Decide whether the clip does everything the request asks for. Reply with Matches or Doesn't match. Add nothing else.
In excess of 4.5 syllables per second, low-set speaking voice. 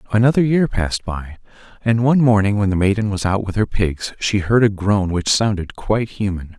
Matches